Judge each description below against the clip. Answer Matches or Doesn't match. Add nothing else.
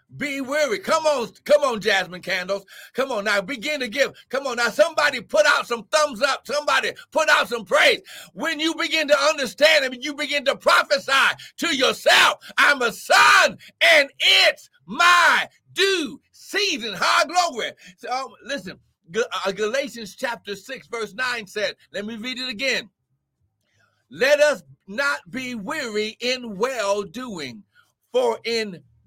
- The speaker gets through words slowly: Doesn't match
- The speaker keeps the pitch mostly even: Doesn't match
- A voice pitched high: Matches